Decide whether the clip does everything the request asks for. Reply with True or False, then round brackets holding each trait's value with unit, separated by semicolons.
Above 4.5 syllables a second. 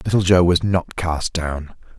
False (4.1 syllables/s)